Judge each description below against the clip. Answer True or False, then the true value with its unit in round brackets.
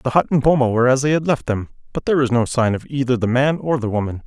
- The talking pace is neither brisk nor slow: False (310 wpm)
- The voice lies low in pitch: True (130 Hz)